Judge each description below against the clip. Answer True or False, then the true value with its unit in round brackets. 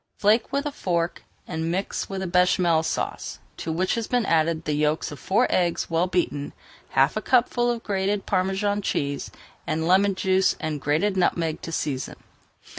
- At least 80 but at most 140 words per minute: False (170 wpm)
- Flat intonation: False (3.9 semitones)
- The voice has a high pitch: False (180 Hz)